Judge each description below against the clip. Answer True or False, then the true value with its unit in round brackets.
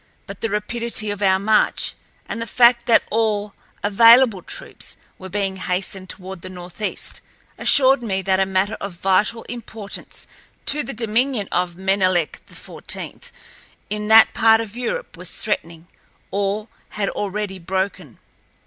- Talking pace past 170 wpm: False (140 wpm)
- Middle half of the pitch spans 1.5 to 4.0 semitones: True (3.2 semitones)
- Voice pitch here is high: True (205 Hz)